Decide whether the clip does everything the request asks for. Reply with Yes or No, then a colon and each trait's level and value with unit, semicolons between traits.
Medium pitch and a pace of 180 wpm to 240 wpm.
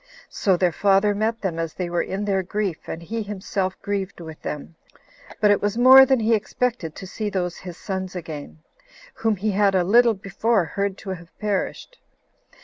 No: high, 195 Hz; average, 190 wpm